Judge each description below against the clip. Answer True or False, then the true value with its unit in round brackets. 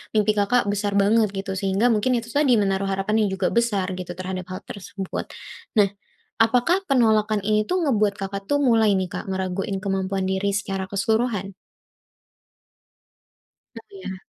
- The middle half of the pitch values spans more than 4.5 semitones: False (2.7 semitones)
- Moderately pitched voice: False (205 Hz)